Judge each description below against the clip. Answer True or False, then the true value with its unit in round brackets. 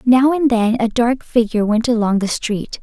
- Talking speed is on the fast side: True (210 wpm)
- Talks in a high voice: True (235 Hz)